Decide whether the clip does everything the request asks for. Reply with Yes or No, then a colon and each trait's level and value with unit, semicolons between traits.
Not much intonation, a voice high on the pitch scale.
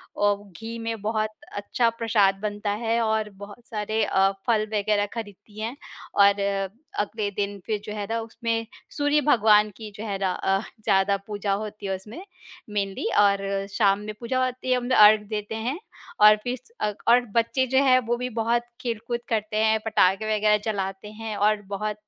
Yes: narrow, 2.0 semitones; high, 215 Hz